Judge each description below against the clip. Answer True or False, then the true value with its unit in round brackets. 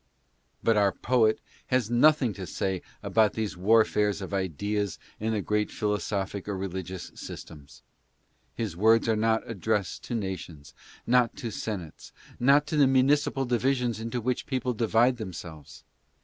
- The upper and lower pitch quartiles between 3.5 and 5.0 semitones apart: True (3.9 semitones)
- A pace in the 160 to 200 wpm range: False (145 wpm)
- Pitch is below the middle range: True (110 Hz)